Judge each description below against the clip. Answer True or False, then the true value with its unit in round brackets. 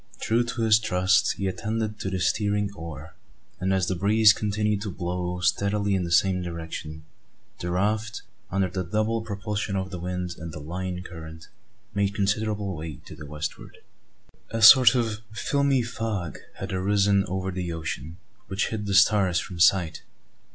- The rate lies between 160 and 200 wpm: True (165 wpm)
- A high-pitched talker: False (95 Hz)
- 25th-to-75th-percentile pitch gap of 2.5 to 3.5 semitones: True (3.1 semitones)